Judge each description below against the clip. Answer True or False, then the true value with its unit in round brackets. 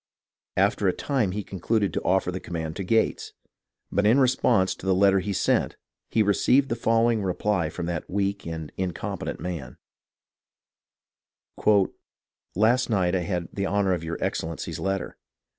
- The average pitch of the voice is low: True (95 Hz)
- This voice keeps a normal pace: True (160 wpm)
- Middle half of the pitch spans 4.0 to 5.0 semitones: False (3.0 semitones)